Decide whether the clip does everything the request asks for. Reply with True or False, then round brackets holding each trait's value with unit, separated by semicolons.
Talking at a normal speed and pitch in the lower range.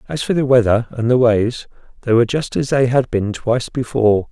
False (220 wpm; 120 Hz)